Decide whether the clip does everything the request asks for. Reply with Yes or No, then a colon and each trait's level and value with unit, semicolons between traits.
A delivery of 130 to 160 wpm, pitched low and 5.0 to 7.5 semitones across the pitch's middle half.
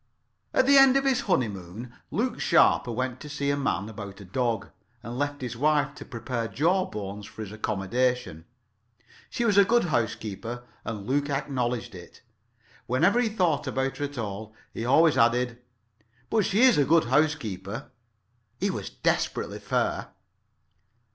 Yes: average, 155 wpm; low, 125 Hz; average, 5.3 semitones